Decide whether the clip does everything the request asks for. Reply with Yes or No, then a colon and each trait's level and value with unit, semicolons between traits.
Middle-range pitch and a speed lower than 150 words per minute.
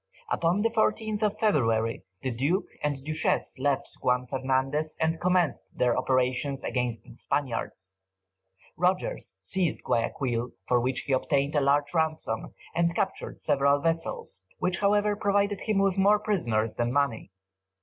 Yes: medium, 145 Hz; average, 140 wpm